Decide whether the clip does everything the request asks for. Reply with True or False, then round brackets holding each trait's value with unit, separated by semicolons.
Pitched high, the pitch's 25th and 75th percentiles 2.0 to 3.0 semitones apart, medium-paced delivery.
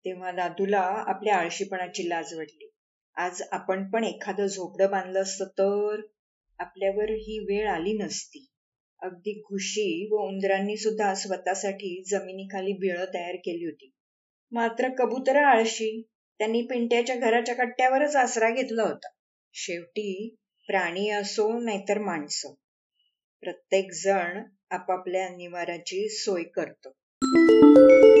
True (195 Hz; 2.7 semitones; 110 wpm)